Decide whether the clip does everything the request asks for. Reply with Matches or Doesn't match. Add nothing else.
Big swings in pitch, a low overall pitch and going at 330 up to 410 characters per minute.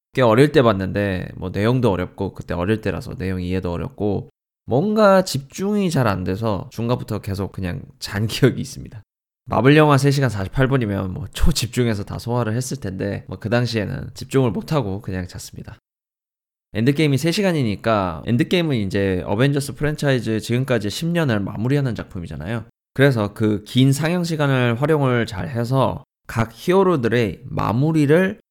Matches